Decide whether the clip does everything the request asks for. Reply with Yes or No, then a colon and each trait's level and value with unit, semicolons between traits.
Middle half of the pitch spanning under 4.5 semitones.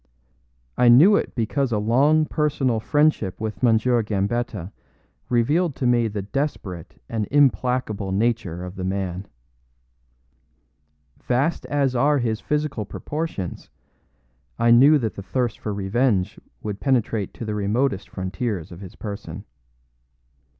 No: average, 4.9 semitones